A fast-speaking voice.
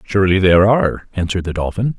No: average, 180 wpm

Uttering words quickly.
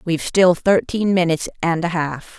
No: average, 175 wpm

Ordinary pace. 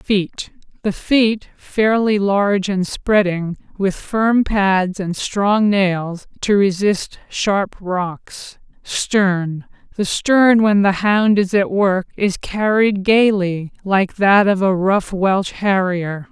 No: slow, 125 wpm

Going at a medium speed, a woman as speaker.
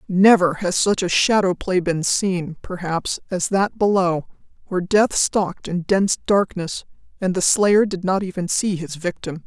Yes: average, 170 wpm; female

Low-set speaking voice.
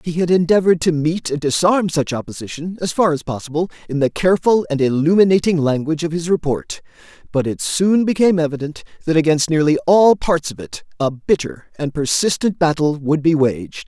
No: medium, 160 Hz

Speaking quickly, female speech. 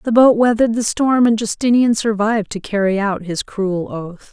No: average, 195 wpm; female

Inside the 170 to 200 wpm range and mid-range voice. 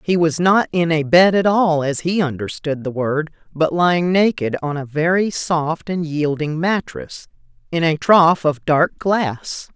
Yes: average, 180 wpm; medium, 165 Hz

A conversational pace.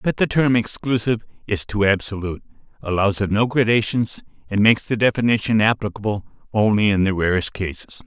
Yes: average, 155 wpm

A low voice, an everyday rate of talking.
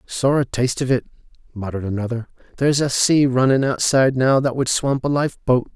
Yes: low, 130 Hz; average, 190 wpm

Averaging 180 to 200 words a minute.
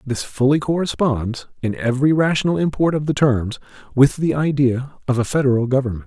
No: average, 170 wpm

